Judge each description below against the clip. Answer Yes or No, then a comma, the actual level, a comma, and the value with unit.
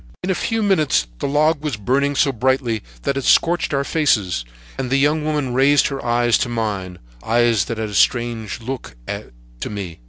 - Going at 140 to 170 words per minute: No, average, 185 wpm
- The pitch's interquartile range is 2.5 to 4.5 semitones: No, average, 4.9 semitones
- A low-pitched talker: Yes, low, 125 Hz